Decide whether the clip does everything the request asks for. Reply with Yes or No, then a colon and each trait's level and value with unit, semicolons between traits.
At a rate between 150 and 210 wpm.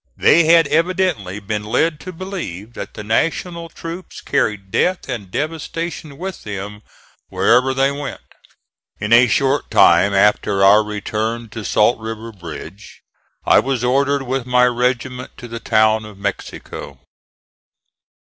No: average, 140 wpm